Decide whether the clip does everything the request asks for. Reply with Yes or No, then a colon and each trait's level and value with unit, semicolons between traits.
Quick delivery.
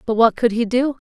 Yes: fast, 280 wpm